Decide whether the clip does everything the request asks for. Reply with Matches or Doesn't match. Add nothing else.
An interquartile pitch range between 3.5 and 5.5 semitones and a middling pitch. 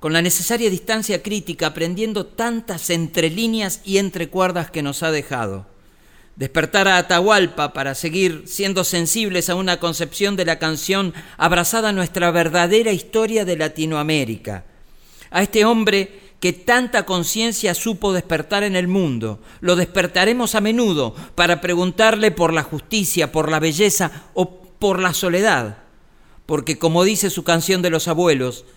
Matches